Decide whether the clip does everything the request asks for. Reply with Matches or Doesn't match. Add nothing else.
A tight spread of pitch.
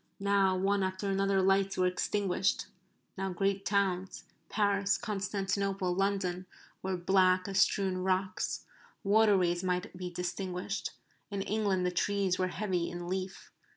Matches